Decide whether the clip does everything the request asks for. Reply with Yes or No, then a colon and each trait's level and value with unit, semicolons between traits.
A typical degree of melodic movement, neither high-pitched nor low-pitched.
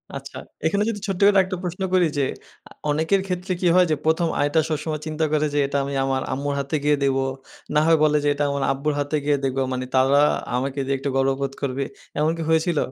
Yes: average, 3.0 semitones; medium, 150 Hz